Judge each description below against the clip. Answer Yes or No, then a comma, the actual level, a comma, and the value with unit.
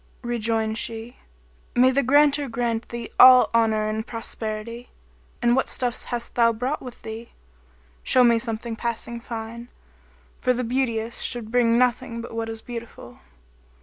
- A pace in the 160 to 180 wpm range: No, average, 150 wpm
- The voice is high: Yes, high, 235 Hz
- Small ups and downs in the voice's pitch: Yes, narrow, 1.6 semitones